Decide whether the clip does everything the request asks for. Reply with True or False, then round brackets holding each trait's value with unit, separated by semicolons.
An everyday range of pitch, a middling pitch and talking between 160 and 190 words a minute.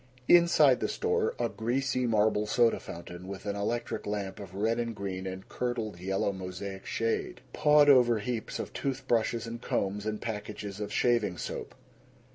False (3.6 semitones; 110 Hz; 165 wpm)